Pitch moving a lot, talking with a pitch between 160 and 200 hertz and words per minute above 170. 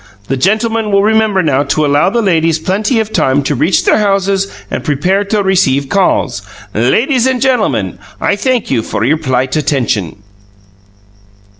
No: wide, 7.1 semitones; high, 190 Hz; average, 160 wpm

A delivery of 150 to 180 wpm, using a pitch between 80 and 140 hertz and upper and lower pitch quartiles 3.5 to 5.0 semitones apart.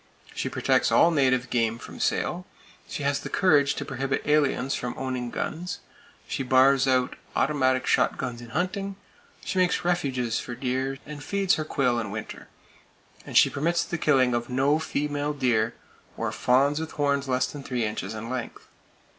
No: average, 170 wpm; low, 135 Hz; average, 3.0 semitones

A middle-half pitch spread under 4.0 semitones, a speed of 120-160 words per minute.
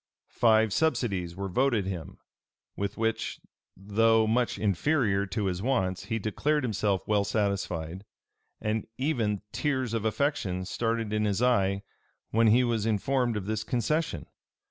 Yes: average, 3.5 semitones; average, 140 wpm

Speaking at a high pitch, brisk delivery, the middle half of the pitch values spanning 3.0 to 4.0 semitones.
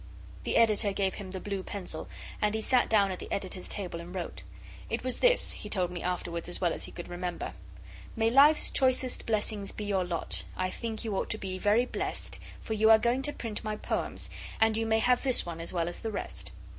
Yes: high, 205 Hz; fast, 230 wpm; average, 3.4 semitones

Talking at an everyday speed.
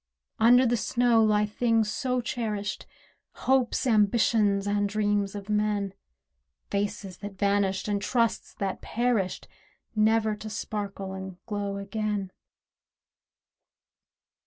No: slow, 110 wpm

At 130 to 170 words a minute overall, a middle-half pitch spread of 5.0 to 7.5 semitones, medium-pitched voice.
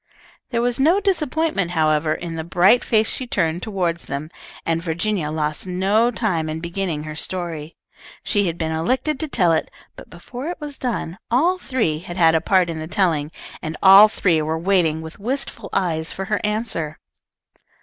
No: average, 180 wpm; wide, 5.6 semitones; medium, 180 Hz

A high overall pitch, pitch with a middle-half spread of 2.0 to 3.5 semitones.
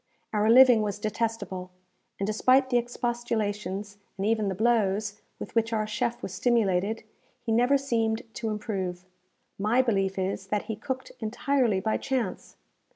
Yes: high, 220 Hz; average, 2.9 semitones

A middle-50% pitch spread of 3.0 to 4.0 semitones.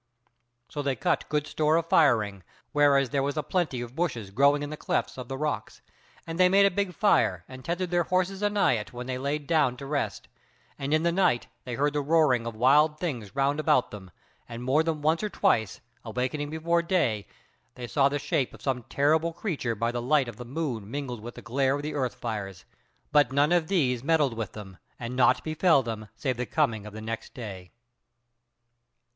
No: average, 4.8 semitones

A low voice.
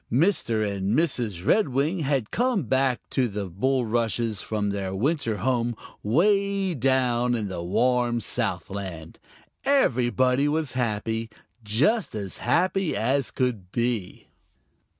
Yes: low, 120 Hz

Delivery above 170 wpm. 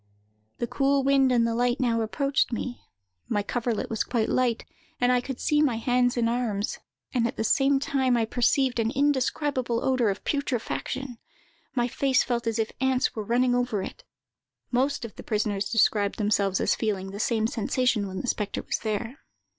Yes: average, 185 wpm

